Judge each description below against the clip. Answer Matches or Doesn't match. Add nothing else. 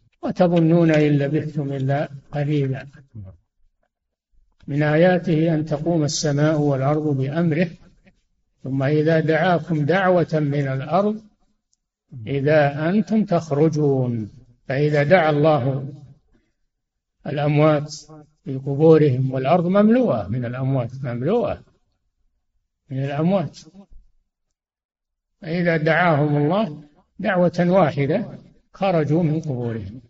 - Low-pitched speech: Doesn't match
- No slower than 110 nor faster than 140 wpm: Doesn't match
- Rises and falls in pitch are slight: Doesn't match